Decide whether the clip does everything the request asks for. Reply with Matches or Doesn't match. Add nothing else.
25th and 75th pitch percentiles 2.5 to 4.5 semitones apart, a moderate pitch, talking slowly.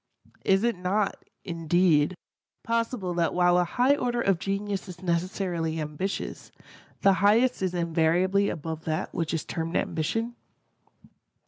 Matches